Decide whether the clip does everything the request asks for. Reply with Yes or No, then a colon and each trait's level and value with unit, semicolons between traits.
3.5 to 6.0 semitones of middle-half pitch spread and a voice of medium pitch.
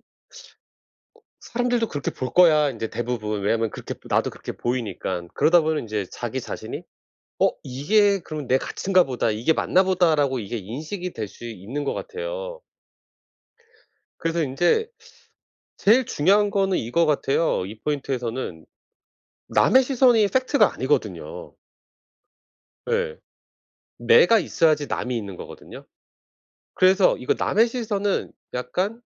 No: wide, 8.9 semitones; medium, 155 Hz